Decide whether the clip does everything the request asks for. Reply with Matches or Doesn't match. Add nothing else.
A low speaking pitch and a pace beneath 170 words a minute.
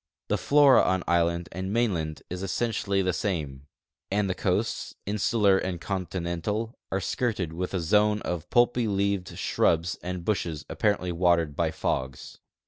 Matches